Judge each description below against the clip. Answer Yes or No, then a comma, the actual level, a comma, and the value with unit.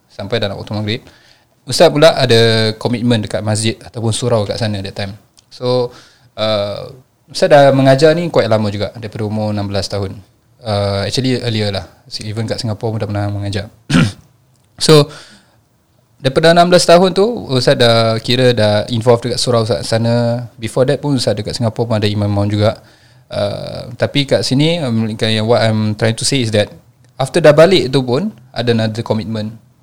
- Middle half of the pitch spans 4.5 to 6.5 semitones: No, average, 3.0 semitones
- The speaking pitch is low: Yes, low, 115 Hz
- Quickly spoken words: Yes, fast, 170 wpm